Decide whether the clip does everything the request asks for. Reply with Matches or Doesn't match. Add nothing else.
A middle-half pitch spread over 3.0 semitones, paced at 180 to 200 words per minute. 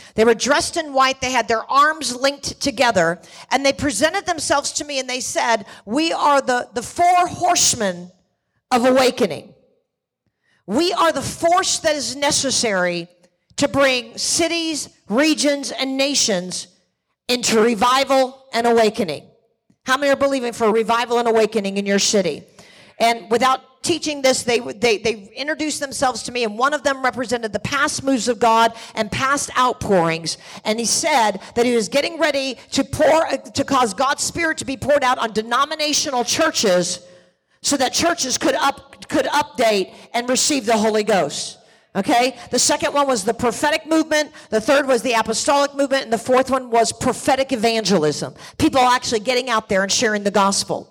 Doesn't match